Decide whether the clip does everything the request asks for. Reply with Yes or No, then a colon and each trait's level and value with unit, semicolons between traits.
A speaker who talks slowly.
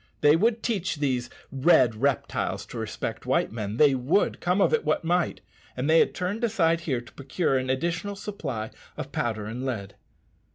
No: average, 180 wpm